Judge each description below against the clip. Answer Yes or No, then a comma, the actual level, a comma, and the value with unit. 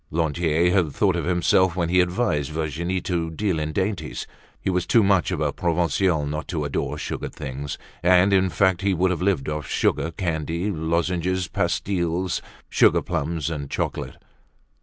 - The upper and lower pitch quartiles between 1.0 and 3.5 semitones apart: Yes, narrow, 2.6 semitones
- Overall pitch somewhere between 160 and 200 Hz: No, very low, 85 Hz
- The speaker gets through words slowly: No, average, 165 wpm